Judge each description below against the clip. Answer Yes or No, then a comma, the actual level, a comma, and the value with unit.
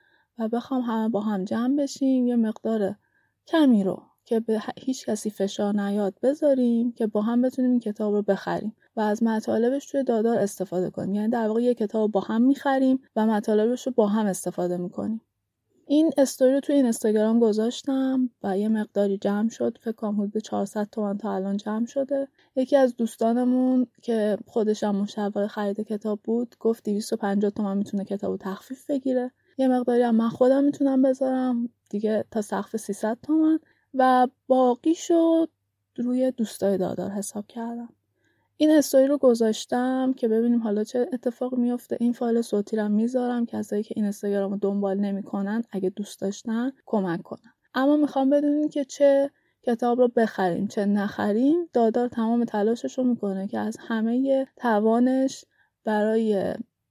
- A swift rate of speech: Yes, fast, 160 wpm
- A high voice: Yes, high, 230 Hz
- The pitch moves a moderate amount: Yes, average, 3.7 semitones